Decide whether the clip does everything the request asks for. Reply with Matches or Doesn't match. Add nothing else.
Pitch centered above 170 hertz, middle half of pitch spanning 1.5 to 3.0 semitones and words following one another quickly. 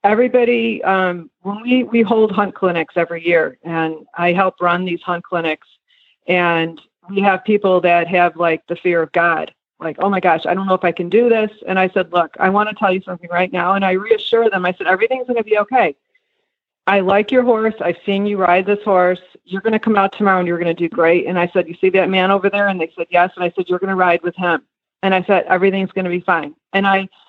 Matches